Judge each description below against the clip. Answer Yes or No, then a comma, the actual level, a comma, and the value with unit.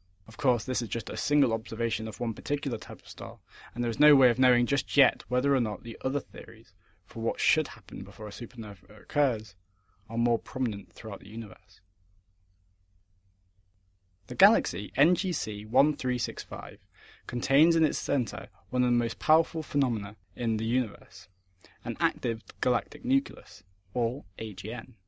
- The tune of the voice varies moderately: Yes, average, 4.7 semitones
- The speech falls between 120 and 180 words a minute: Yes, average, 160 wpm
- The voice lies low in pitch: Yes, low, 115 Hz